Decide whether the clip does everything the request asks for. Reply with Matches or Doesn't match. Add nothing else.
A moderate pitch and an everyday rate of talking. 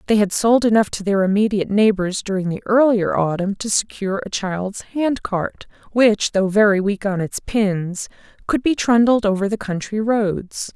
Doesn't match